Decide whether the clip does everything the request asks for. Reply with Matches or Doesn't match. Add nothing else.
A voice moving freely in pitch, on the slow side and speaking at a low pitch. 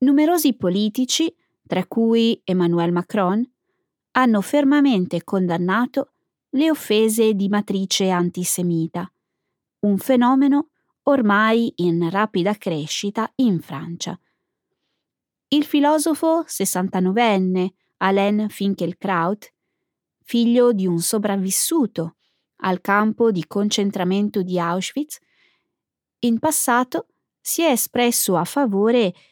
Doesn't match